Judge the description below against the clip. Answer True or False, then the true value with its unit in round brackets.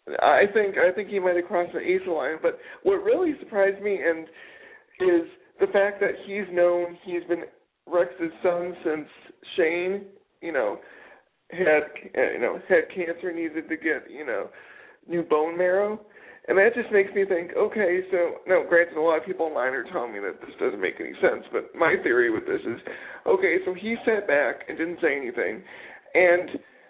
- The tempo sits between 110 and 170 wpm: False (185 wpm)